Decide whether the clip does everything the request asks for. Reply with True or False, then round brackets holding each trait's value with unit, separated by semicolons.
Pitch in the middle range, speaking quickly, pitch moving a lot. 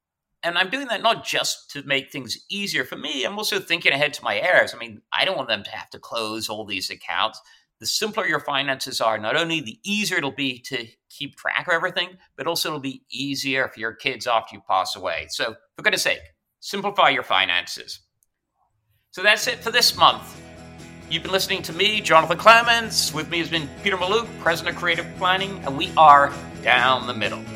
True (150 Hz; 210 wpm; 8.0 semitones)